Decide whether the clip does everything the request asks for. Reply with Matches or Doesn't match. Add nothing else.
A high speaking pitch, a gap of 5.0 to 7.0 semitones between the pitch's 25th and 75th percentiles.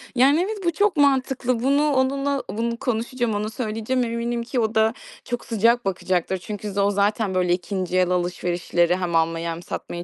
Matches